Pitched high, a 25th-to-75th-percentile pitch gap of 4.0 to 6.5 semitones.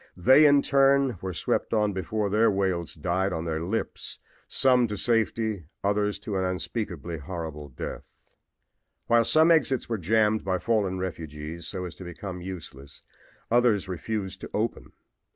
No: very low, 95 Hz; average, 4.5 semitones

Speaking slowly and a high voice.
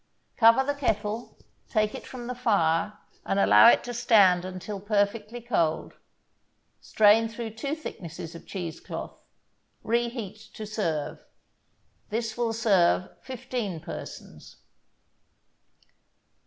Yes: slow, 115 wpm; high, 215 Hz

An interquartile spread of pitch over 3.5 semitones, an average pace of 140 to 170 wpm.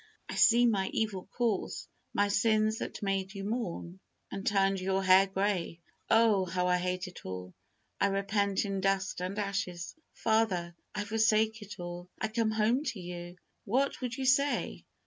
No: average, 3.0 semitones; average, 165 wpm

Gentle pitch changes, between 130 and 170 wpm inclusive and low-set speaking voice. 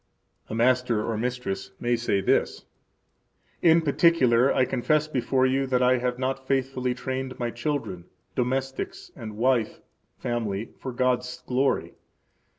Yes: narrow, 1.9 semitones; slow, 135 wpm; low, 125 Hz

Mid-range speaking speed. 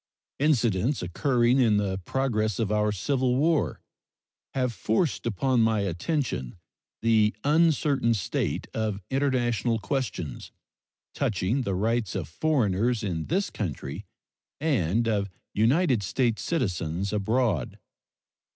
No: slow, 110 wpm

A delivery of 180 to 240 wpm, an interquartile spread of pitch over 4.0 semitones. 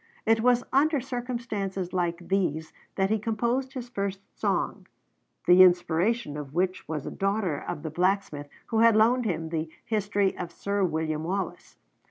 No: average, 160 wpm; average, 5.0 semitones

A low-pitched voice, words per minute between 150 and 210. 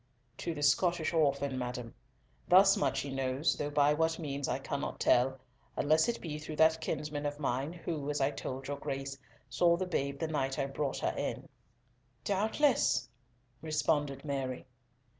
No: medium, 145 Hz; average, 165 wpm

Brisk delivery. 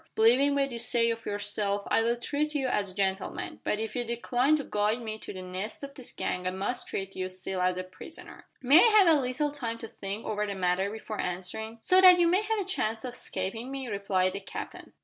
Yes: fast, 240 wpm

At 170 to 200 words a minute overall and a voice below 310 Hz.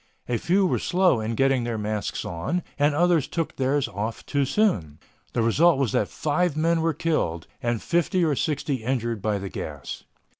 Yes: average, 185 wpm; low, 135 Hz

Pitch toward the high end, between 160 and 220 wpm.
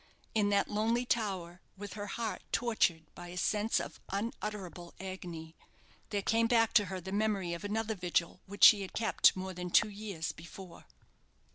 Yes: high, 200 Hz; average, 170 wpm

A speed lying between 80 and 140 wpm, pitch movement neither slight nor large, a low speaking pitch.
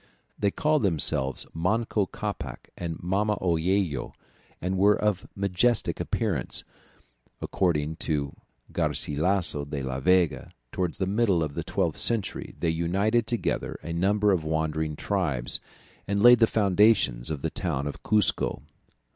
Yes: slow, 135 wpm; average, 4.9 semitones; very low, 90 Hz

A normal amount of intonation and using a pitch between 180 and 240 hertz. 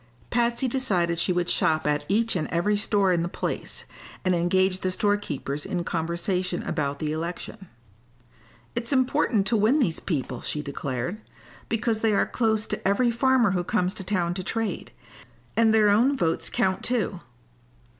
Yes: average, 4.7 semitones; high, 190 Hz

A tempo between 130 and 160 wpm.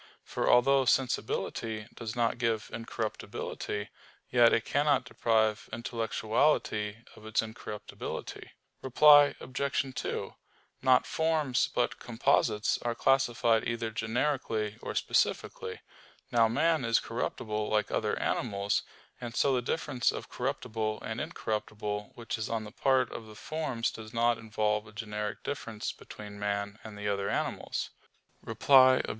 Yes: slow, 135 wpm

